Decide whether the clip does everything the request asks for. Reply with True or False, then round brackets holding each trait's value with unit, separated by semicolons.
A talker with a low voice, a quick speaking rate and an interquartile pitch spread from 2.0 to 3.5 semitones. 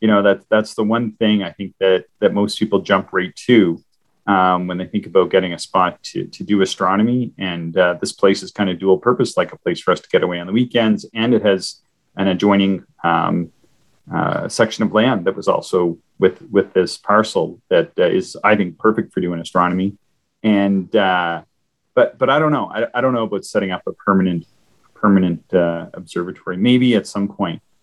True (100 Hz; 210 wpm; 2.9 semitones)